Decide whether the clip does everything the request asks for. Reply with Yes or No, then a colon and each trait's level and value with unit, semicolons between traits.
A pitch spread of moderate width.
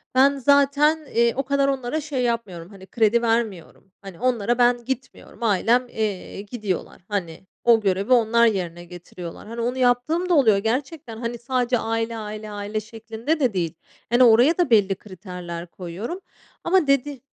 Yes: average, 4.2 semitones